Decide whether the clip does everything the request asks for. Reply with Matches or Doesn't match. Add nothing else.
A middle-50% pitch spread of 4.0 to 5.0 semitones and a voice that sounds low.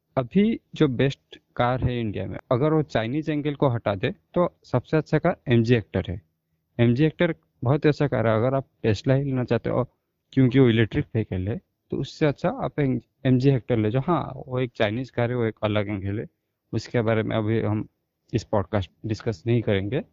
Matches